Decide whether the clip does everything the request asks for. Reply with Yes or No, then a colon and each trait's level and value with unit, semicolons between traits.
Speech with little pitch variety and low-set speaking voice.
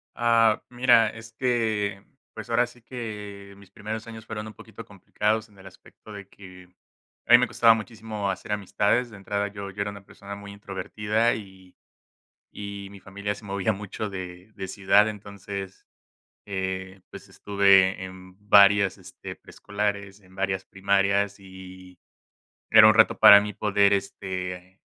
Yes: narrow, 1.9 semitones; low, 100 Hz